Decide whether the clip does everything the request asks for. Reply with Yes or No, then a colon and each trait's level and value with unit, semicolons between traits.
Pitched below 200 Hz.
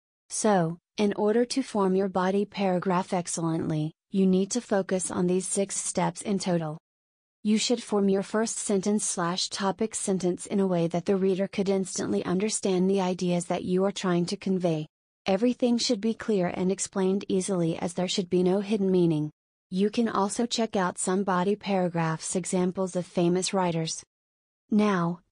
Yes: high, 190 Hz